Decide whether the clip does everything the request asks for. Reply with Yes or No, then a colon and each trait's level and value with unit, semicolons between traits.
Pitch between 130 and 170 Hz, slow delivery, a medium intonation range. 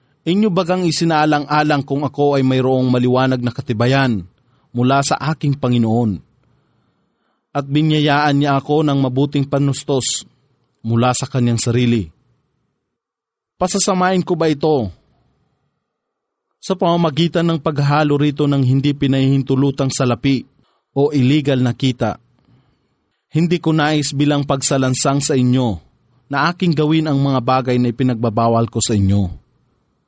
Yes: medium, 140 Hz; slow, 120 wpm; average, 3.2 semitones